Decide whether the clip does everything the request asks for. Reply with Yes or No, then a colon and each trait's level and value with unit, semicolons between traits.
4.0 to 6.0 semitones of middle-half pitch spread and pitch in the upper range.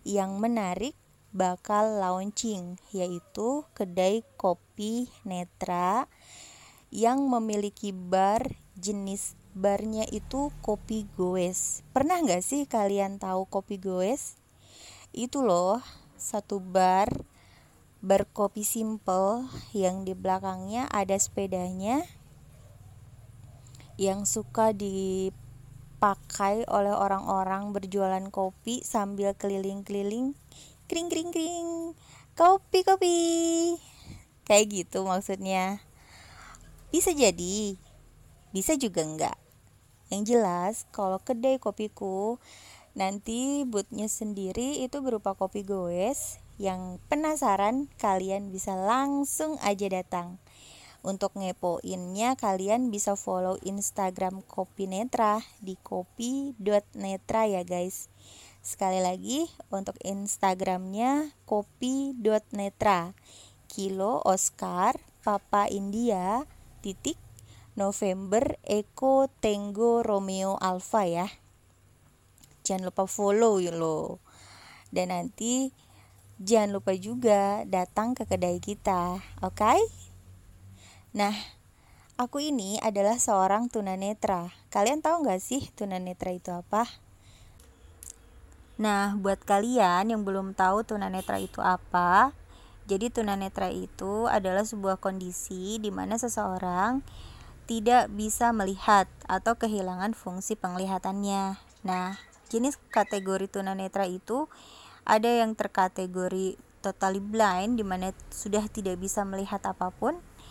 No: average, 3.0 semitones; high, 200 Hz